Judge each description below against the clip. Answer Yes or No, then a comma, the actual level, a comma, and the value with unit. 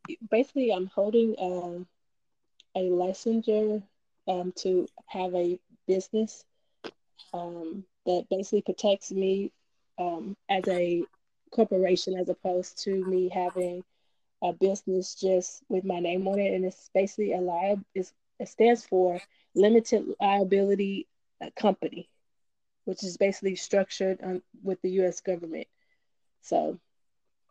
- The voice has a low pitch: No, high, 190 Hz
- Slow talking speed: Yes, slow, 120 wpm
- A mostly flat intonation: Yes, narrow, 1.8 semitones